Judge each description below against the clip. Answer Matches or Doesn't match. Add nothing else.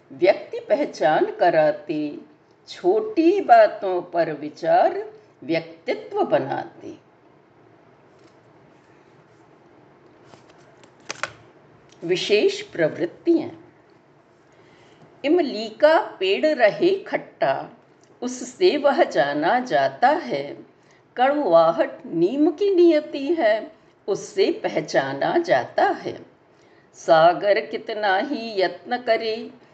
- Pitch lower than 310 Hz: Doesn't match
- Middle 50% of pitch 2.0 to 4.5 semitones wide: Doesn't match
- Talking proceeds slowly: Matches